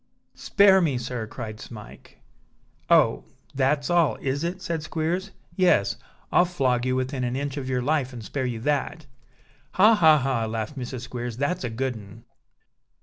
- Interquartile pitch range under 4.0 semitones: No, average, 4.5 semitones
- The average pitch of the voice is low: Yes, low, 130 Hz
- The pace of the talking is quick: No, average, 165 wpm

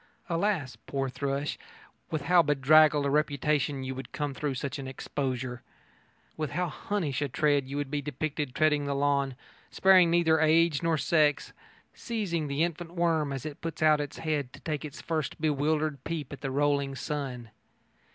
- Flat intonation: Yes, narrow, 2.3 semitones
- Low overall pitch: No, medium, 145 Hz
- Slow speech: No, average, 170 wpm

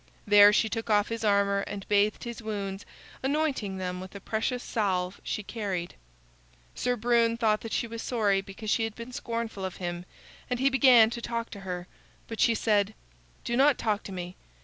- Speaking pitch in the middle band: No, high, 215 Hz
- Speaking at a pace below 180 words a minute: No, average, 195 wpm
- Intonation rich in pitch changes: No, average, 2.9 semitones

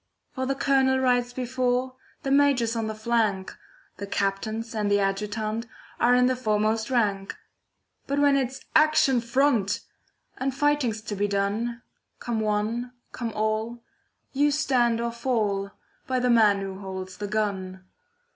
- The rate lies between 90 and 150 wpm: Yes, average, 145 wpm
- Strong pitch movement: No, average, 3.6 semitones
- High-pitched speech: Yes, high, 230 Hz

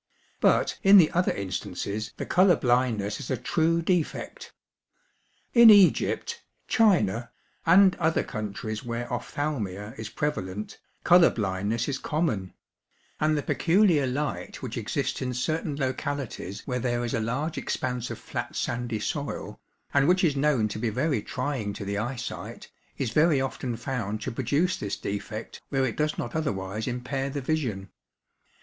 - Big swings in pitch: Yes, wide, 5.9 semitones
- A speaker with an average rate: Yes, average, 150 wpm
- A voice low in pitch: Yes, low, 130 Hz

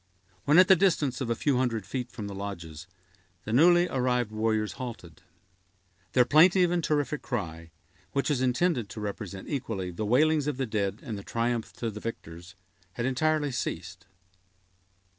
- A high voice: No, low, 120 Hz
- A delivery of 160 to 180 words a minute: Yes, average, 165 wpm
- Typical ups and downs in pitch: No, wide, 6.2 semitones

